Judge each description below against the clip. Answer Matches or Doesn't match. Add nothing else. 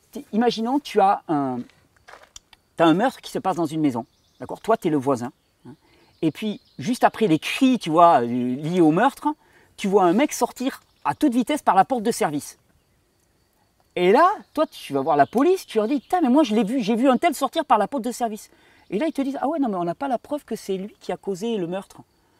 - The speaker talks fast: Matches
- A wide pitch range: Matches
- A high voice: Matches